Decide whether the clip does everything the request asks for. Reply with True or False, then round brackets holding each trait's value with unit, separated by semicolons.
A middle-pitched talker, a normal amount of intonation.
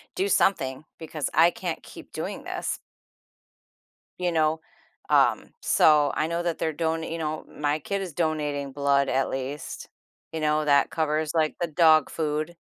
False (155 Hz; 1.8 semitones)